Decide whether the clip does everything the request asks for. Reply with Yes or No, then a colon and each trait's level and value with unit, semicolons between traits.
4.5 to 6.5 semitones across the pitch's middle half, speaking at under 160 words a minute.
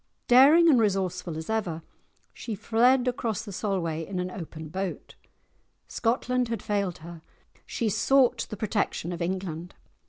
Yes: average, 5.1 semitones; average, 145 wpm